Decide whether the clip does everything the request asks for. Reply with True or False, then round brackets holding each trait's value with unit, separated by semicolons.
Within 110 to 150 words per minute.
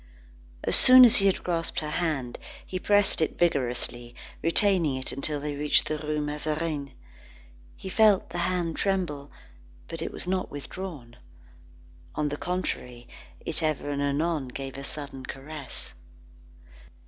True (145 wpm)